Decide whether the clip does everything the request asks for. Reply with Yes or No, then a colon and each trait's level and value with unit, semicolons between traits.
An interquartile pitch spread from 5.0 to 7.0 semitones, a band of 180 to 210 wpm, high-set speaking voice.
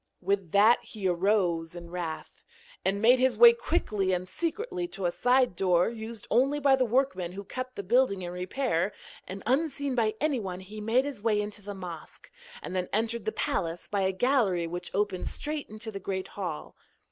Yes: average, 5.3 semitones; average, 190 wpm; high, 205 Hz